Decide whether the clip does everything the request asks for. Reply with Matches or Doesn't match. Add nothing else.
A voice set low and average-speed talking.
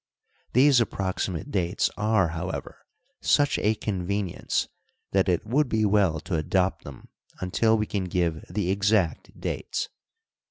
Doesn't match